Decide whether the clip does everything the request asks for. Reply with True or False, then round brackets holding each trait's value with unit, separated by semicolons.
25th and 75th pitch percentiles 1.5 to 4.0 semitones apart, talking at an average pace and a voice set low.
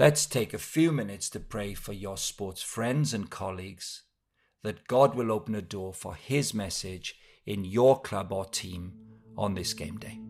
True (3.3 semitones; 180 wpm; 105 Hz)